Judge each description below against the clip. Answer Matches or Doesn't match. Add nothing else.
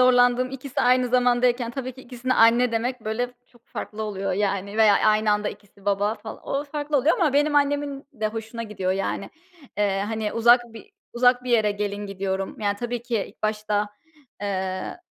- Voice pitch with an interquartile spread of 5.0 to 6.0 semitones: Doesn't match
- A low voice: Doesn't match